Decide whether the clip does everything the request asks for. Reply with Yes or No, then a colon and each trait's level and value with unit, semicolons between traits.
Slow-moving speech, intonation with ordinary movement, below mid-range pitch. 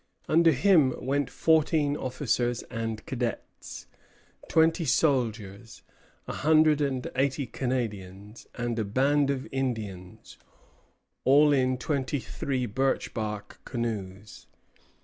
Yes: slow, 105 wpm; average, 4.2 semitones; low, 130 Hz